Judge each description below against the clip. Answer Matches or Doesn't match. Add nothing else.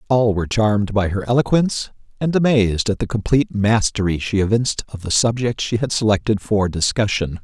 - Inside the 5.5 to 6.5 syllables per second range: Matches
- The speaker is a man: Matches